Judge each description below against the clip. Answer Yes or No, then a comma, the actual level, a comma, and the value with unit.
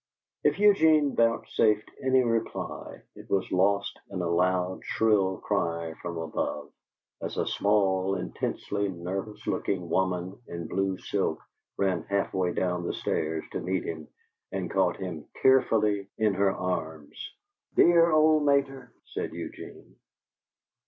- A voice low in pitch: Yes, very low, 95 Hz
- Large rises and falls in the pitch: No, average, 3.7 semitones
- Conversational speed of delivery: No, slow, 130 wpm